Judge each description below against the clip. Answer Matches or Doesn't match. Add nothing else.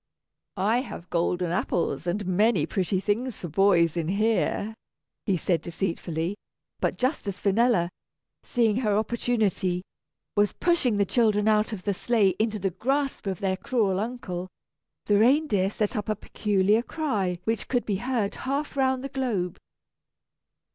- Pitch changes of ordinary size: Matches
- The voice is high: Matches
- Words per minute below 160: Matches